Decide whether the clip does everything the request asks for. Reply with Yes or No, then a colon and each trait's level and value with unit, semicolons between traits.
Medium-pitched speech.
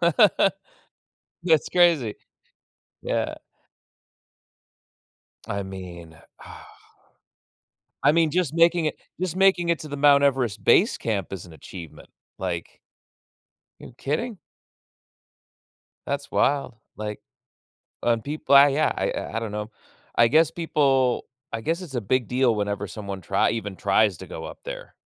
No: low, 130 Hz